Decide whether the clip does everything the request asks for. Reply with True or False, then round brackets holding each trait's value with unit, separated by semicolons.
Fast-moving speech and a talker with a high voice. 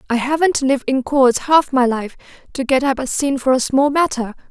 True (225 wpm; 265 Hz)